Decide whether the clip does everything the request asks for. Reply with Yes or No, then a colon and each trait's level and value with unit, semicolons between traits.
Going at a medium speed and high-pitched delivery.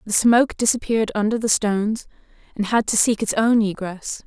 Yes: average, 185 wpm; high, 215 Hz